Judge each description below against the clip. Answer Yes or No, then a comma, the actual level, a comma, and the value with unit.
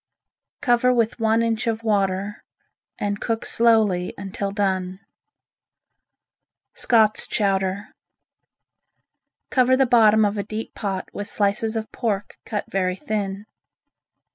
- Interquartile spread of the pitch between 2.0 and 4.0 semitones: Yes, narrow, 2.4 semitones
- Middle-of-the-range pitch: No, high, 210 Hz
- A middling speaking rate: No, slow, 115 wpm